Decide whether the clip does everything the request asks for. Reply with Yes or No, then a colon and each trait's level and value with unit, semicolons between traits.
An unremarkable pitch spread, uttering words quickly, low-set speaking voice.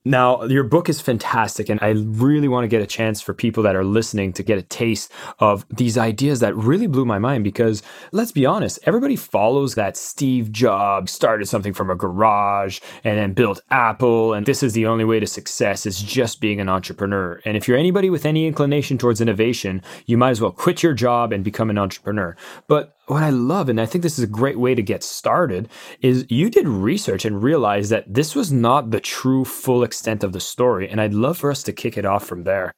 Yes: average, 3.8 semitones; fast, 225 wpm; low, 115 Hz